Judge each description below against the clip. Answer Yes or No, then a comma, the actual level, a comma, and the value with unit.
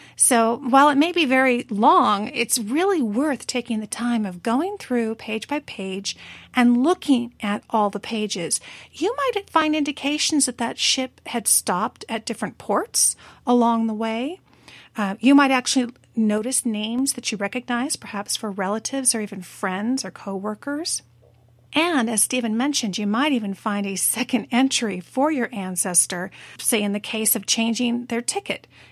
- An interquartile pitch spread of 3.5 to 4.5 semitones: Yes, average, 4.0 semitones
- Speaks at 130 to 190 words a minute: Yes, average, 165 wpm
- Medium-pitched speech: No, high, 235 Hz